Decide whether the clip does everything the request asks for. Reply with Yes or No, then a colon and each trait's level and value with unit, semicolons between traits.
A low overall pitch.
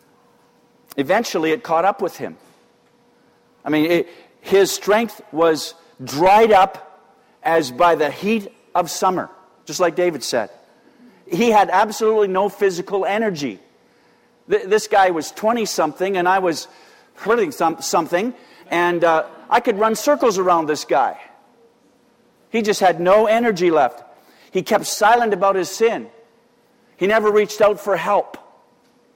No: high, 195 Hz